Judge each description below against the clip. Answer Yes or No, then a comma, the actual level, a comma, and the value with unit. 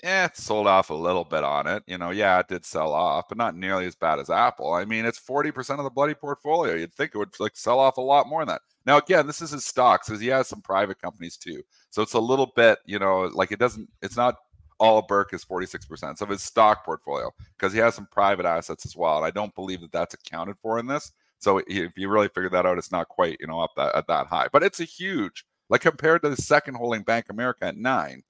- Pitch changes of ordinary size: No, wide, 6.6 semitones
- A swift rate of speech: Yes, fast, 270 wpm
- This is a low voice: Yes, low, 115 Hz